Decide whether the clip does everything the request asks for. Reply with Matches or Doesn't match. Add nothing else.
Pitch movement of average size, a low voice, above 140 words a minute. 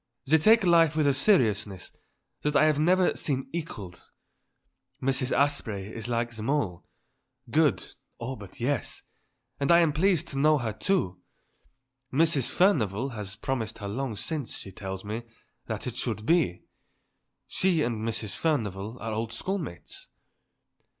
Doesn't match